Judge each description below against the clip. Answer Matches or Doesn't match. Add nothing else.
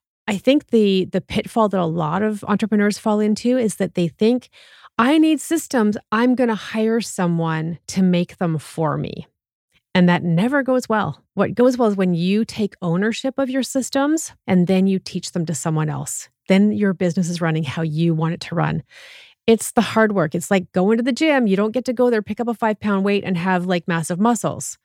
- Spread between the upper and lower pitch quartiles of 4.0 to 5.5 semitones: Matches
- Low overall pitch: Doesn't match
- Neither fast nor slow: Doesn't match